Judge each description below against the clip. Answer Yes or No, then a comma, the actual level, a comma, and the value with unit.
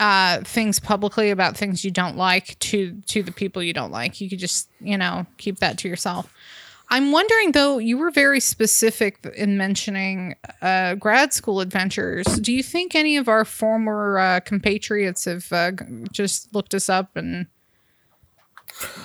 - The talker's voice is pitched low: No, high, 200 Hz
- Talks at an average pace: Yes, average, 165 wpm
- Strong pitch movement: No, average, 2.9 semitones